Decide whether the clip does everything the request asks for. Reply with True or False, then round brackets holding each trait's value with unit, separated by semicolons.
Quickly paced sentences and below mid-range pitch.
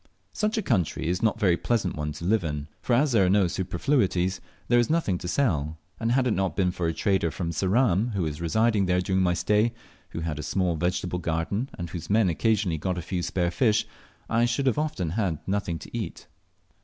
True (225 wpm; 95 Hz)